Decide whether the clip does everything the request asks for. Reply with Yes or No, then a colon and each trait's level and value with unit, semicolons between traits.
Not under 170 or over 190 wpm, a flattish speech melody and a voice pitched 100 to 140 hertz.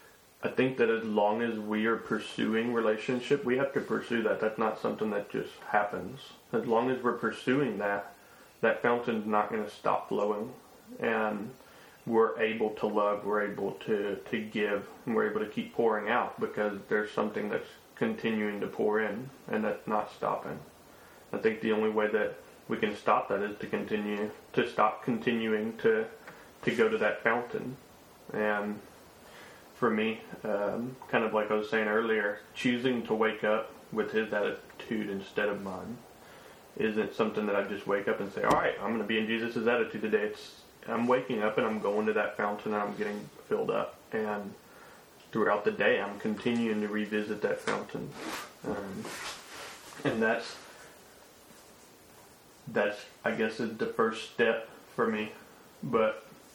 Yes: average, 175 wpm; narrow, 1.5 semitones; low, 110 Hz